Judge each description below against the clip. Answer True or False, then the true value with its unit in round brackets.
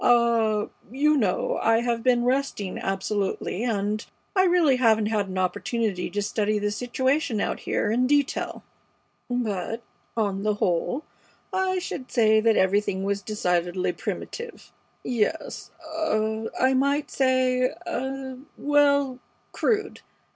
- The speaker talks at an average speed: False (125 wpm)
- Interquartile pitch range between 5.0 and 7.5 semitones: False (4.4 semitones)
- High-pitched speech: True (235 Hz)